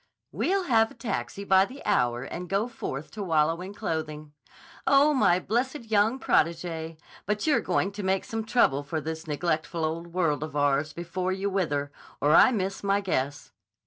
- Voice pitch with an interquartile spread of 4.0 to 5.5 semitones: Yes, average, 5.1 semitones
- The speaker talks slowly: No, average, 175 wpm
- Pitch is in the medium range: Yes, medium, 180 Hz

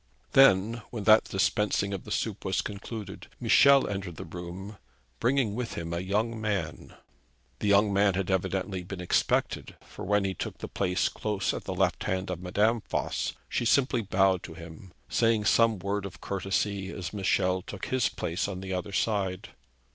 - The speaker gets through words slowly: No, average, 175 wpm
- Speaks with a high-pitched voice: No, low, 100 Hz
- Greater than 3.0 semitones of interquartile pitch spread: No, narrow, 2.4 semitones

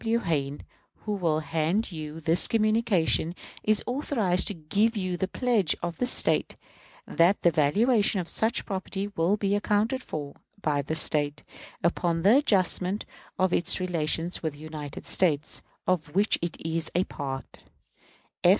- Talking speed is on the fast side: No, average, 150 wpm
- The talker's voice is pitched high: No, medium, 180 Hz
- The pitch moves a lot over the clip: No, average, 4.7 semitones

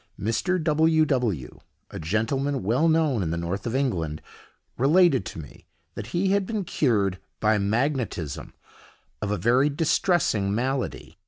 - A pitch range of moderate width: No, wide, 7.6 semitones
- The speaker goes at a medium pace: Yes, average, 145 wpm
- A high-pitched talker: No, low, 125 Hz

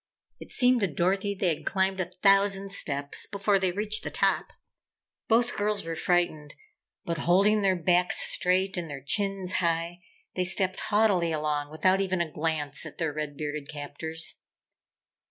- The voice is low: No, medium, 180 Hz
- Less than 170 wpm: Yes, average, 160 wpm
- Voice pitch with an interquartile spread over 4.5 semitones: No, average, 3.7 semitones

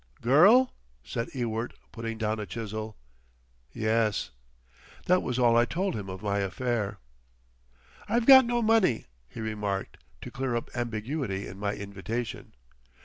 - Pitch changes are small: No, average, 3.9 semitones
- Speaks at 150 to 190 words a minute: No, average, 140 wpm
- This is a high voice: No, low, 115 Hz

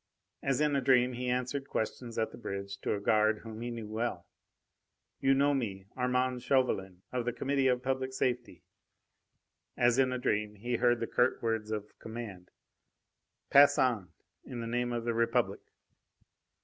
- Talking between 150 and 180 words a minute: Yes, average, 170 wpm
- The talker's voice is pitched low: Yes, low, 120 Hz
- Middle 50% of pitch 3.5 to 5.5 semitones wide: No, narrow, 2.6 semitones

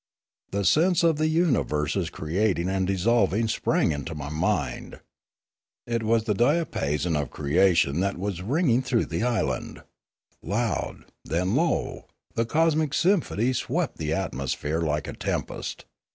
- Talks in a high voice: No, low, 100 Hz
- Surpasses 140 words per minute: No, slow, 135 wpm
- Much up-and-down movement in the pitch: Yes, wide, 7.2 semitones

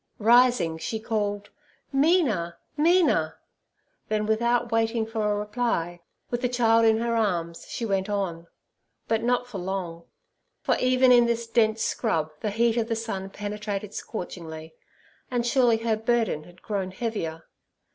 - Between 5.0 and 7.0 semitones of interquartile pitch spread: No, average, 3.6 semitones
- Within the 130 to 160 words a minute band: Yes, average, 145 wpm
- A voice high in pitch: Yes, high, 220 Hz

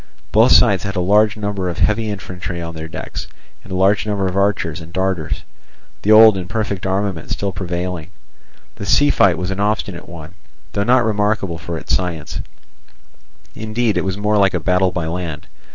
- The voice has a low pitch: Yes, very low, 95 Hz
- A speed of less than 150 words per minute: No, average, 185 wpm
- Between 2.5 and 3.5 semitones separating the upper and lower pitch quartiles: Yes, average, 2.8 semitones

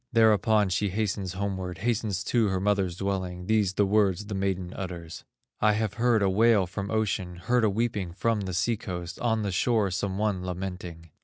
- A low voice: Yes, low, 100 Hz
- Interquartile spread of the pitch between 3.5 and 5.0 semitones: No, average, 2.8 semitones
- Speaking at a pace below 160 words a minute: No, average, 185 wpm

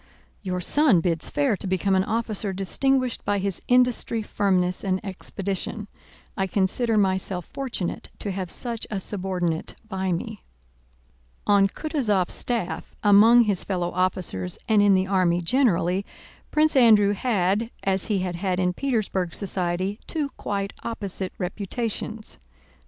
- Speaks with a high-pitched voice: Yes, high, 195 Hz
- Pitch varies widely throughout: No, average, 3.3 semitones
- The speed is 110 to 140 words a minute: Yes, slow, 135 wpm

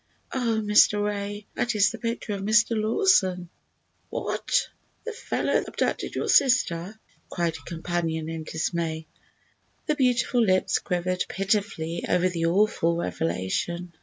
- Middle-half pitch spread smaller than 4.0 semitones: No, average, 4.4 semitones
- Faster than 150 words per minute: No, slow, 135 wpm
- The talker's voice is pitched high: Yes, high, 195 Hz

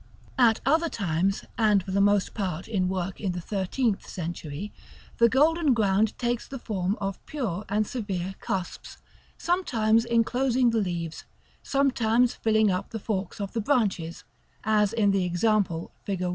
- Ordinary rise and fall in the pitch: Yes, average, 3.7 semitones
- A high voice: Yes, high, 210 Hz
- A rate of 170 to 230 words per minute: No, average, 155 wpm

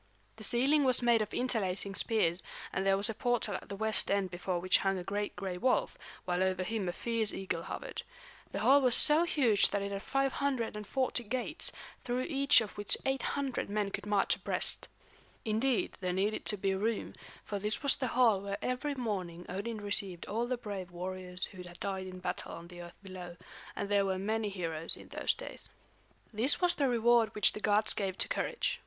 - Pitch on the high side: Yes, high, 205 Hz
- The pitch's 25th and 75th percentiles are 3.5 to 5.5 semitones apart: Yes, average, 4.2 semitones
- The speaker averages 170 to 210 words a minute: Yes, average, 200 wpm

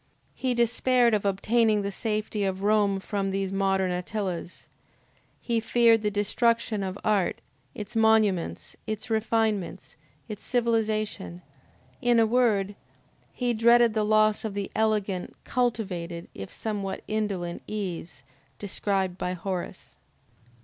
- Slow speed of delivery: Yes, slow, 120 wpm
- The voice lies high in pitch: Yes, high, 210 Hz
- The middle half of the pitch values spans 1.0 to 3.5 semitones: Yes, narrow, 2.6 semitones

